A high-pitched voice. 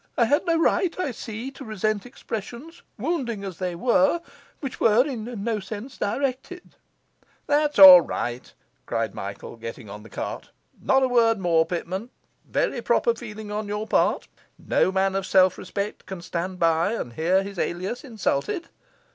Yes: high, 215 Hz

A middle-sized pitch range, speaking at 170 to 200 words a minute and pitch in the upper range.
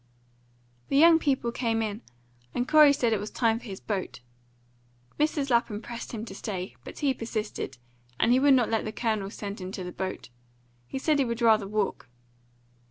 Yes: average, 4.0 semitones; average, 190 wpm; high, 230 Hz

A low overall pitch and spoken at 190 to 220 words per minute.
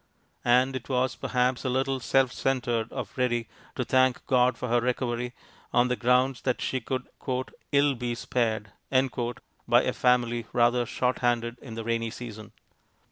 No: low, 125 Hz; average, 160 wpm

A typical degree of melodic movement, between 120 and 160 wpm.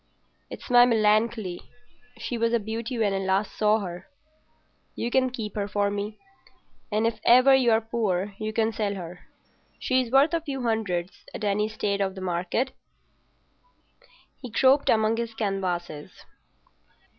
Yes: average, 3.0 semitones; average, 150 wpm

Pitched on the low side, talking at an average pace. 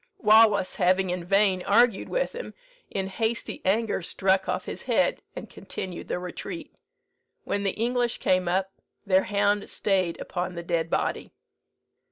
No: high, 195 Hz; average, 150 wpm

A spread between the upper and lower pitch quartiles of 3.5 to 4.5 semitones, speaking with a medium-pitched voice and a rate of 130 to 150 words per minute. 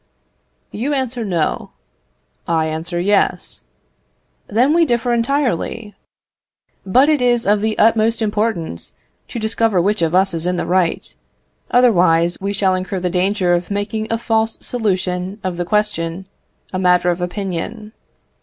No: average, 4.1 semitones; high, 200 Hz; average, 145 wpm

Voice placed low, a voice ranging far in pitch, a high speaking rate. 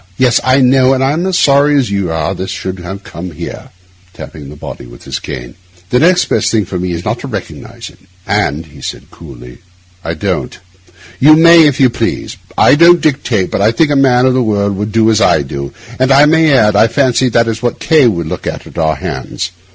Yes: low, 115 Hz; wide, 7.8 semitones; fast, 230 wpm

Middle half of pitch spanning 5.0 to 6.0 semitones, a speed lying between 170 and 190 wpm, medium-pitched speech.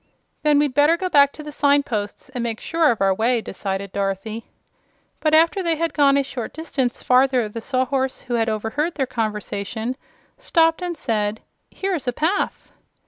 No: wide, 5.4 semitones; average, 180 wpm; very high, 260 Hz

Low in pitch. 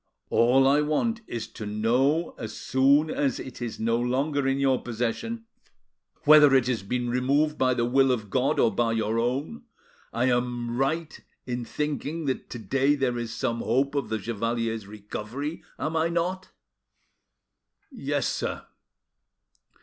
Yes: low, 130 Hz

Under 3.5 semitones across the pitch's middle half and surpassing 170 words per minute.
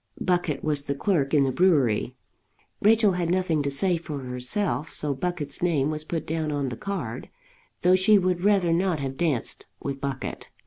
No: average, 4.6 semitones; average, 180 wpm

